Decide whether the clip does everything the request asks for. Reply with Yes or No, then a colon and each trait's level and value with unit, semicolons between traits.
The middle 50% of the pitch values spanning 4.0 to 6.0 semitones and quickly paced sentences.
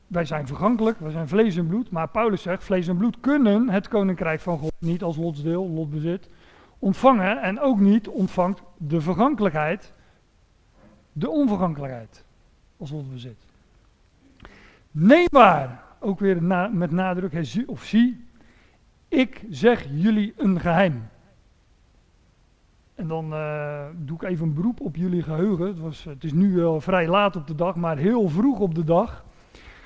No: average, 4.5 semitones; average, 155 wpm